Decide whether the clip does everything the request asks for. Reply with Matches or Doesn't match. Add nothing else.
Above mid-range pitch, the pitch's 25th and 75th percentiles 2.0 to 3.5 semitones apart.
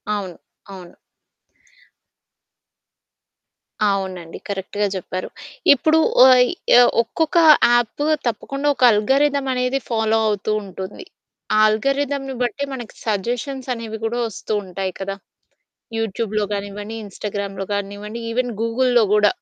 Doesn't match